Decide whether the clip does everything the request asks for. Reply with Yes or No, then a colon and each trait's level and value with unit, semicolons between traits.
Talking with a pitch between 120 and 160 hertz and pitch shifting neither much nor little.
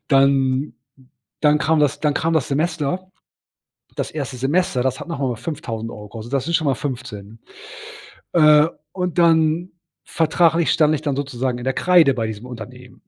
Yes: medium, 140 Hz; average, 4.1 semitones